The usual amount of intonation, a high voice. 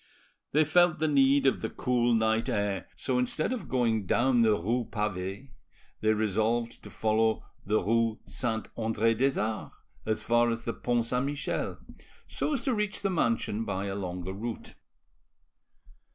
No: average, 3.5 semitones; low, 115 Hz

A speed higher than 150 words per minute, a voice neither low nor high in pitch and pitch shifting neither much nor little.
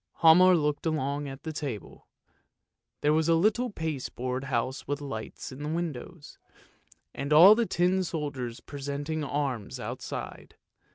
No: average, 145 wpm; medium, 150 Hz; average, 3.2 semitones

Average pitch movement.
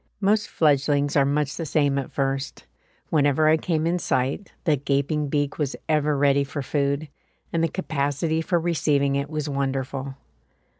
No: narrow, 2.2 semitones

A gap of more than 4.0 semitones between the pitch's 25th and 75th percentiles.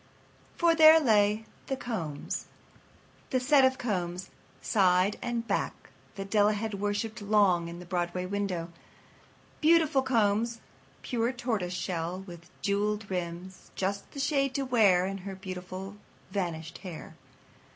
Yes: average, 4.4 semitones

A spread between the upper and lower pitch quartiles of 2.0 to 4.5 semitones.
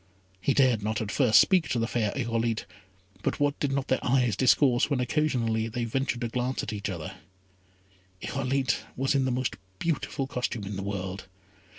Yes: average, 3.5 semitones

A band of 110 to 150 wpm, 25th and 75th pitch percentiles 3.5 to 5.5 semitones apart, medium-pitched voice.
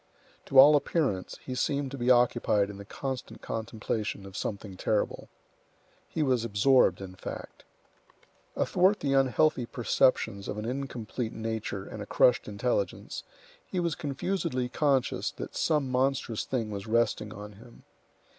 No: average, 145 wpm; average, 4.5 semitones; low, 125 Hz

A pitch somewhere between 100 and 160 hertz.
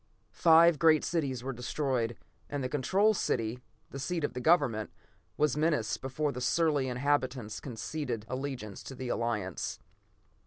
Yes: low, 135 Hz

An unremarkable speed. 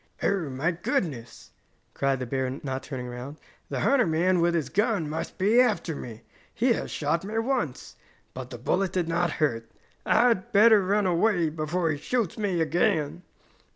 Yes: average, 175 wpm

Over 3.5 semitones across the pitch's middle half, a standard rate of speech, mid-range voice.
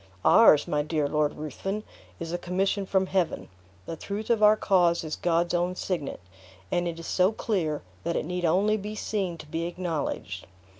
No: average, 3.1 semitones; average, 180 wpm; medium, 175 Hz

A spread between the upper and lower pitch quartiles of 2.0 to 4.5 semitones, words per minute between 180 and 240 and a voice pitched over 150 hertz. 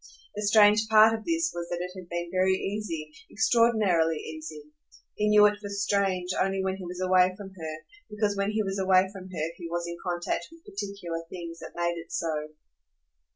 Yes: average, 3.2 semitones; average, 200 wpm; high, 190 Hz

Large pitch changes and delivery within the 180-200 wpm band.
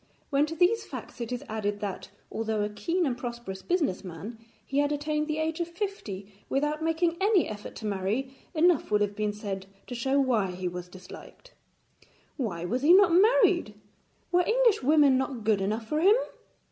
Yes: wide, 7.8 semitones; average, 185 wpm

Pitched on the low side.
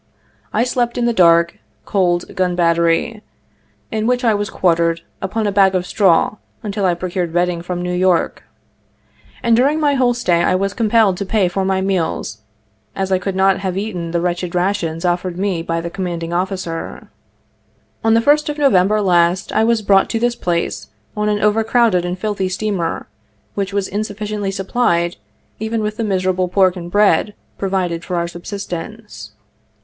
No: high, 190 Hz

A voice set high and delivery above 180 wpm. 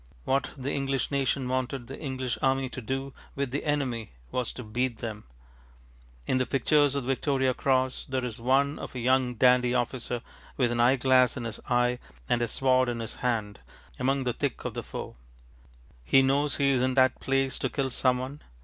No: low, 130 Hz; average, 195 wpm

